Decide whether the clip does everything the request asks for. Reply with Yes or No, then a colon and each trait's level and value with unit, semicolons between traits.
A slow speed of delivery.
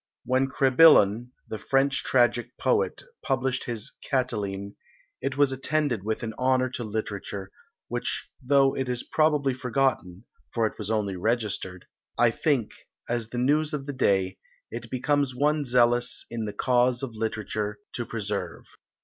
No: average, 150 wpm